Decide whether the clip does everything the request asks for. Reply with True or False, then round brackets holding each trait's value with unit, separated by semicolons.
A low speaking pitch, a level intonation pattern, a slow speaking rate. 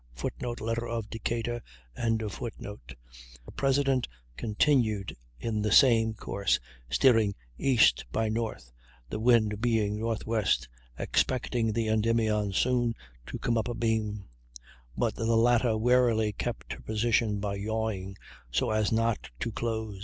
True (110 Hz; 1.9 semitones; 125 wpm)